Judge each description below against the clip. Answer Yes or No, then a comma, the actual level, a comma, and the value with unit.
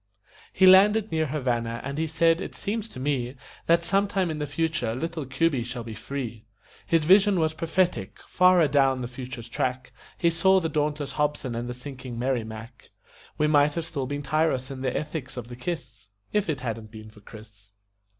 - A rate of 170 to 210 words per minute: Yes, average, 190 wpm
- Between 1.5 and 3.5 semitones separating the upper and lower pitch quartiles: No, average, 5.1 semitones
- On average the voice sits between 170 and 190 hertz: No, medium, 140 Hz